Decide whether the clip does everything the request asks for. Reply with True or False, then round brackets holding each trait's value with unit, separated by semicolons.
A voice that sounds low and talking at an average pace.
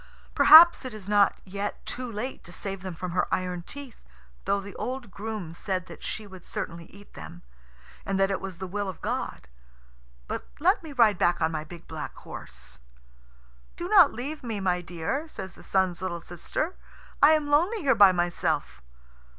False (200 Hz; 185 wpm)